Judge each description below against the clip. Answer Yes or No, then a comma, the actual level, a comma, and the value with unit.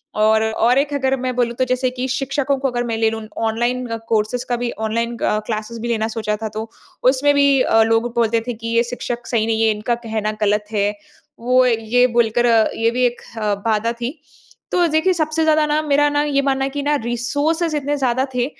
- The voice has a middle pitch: No, high, 240 Hz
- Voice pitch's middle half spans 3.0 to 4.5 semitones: Yes, average, 3.4 semitones